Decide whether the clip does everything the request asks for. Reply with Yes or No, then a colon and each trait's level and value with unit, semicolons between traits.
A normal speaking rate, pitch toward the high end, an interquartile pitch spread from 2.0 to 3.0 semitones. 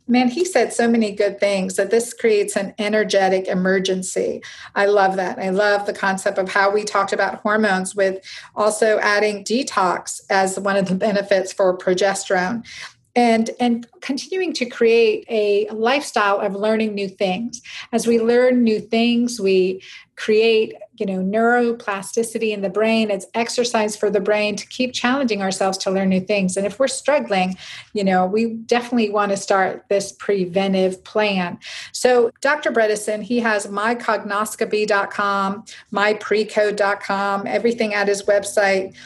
Yes: average, 150 wpm; high, 210 Hz; average, 2.7 semitones